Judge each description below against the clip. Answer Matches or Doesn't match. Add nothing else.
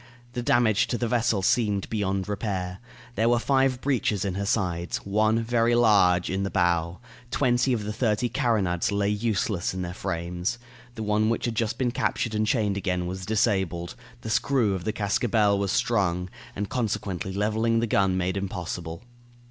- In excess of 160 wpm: Matches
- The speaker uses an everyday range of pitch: Matches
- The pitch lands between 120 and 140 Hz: Doesn't match